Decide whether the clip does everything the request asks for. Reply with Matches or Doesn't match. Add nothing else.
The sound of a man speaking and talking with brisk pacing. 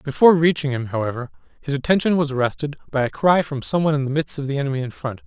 Matches